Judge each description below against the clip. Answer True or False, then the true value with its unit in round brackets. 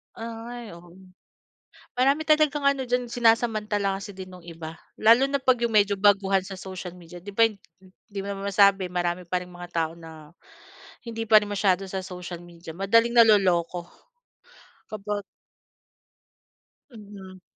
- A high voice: True (200 Hz)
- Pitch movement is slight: False (4.0 semitones)